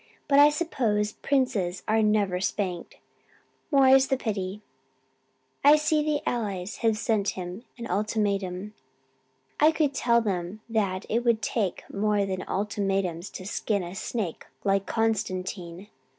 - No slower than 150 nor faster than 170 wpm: No, slow, 135 wpm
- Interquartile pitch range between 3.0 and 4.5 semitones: Yes, average, 3.8 semitones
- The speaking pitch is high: Yes, high, 210 Hz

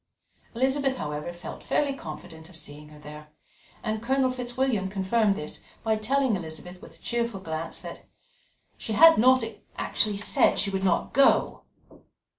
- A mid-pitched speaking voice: No, high, 205 Hz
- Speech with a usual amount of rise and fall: No, wide, 7.5 semitones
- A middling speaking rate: Yes, average, 150 wpm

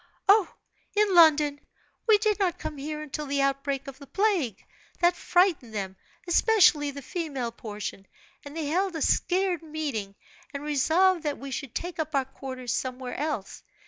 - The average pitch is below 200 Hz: No, very high, 295 Hz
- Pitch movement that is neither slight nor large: Yes, average, 4.7 semitones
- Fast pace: No, average, 165 wpm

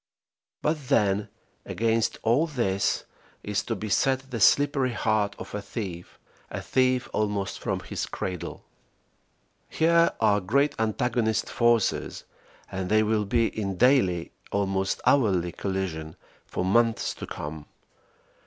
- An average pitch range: Yes, average, 4.4 semitones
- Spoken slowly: Yes, slow, 125 wpm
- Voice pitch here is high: No, low, 110 Hz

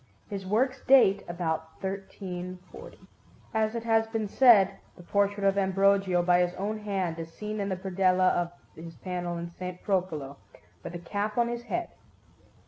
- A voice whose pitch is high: Yes, high, 195 Hz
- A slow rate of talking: No, average, 165 wpm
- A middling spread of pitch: Yes, average, 3.0 semitones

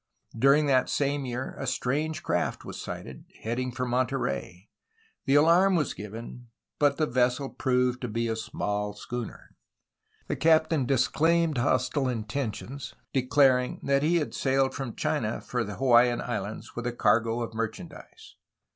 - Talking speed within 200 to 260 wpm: No, average, 150 wpm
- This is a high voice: No, low, 125 Hz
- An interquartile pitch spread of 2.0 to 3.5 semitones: Yes, average, 3.2 semitones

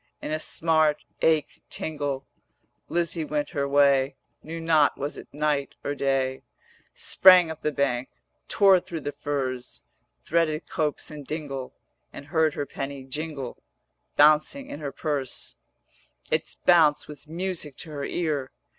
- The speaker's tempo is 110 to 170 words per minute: Yes, average, 145 wpm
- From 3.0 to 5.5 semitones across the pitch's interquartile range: No, narrow, 2.4 semitones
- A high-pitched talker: No, medium, 150 Hz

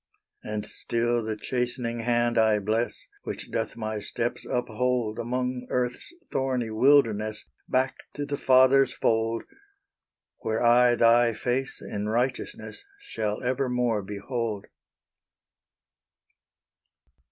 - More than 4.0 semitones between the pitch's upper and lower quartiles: No, narrow, 2.4 semitones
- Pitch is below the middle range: Yes, low, 120 Hz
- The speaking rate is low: Yes, slow, 105 wpm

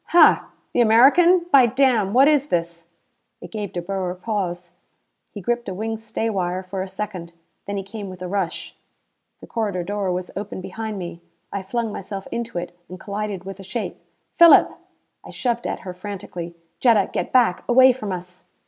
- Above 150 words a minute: Yes, average, 185 wpm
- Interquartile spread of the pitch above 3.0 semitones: Yes, average, 4.1 semitones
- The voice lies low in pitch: No, high, 200 Hz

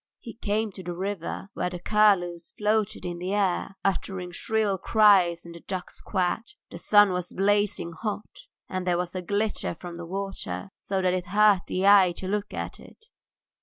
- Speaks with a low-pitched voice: No, high, 190 Hz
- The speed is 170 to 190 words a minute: Yes, average, 185 wpm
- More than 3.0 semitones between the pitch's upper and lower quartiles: No, narrow, 2.6 semitones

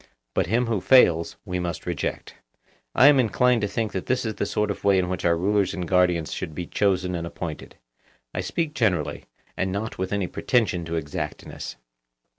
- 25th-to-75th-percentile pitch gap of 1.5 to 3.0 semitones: No, average, 4.0 semitones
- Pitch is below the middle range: Yes, very low, 95 Hz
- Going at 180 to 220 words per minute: Yes, average, 195 wpm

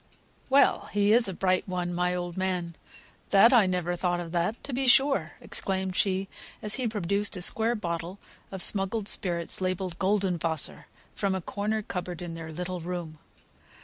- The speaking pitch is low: No, medium, 185 Hz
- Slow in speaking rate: No, average, 175 wpm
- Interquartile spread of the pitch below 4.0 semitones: Yes, average, 2.7 semitones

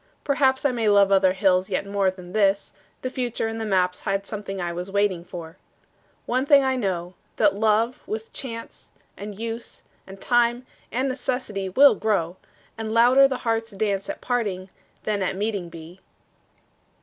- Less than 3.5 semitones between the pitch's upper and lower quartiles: No, average, 3.9 semitones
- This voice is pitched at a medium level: No, high, 210 Hz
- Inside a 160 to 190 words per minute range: Yes, average, 170 wpm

